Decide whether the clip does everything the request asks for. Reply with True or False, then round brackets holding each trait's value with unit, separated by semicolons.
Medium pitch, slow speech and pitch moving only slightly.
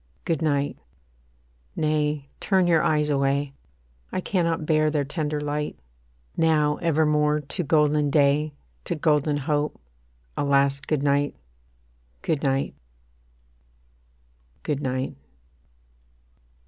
True (150 Hz; 105 wpm; 1.4 semitones)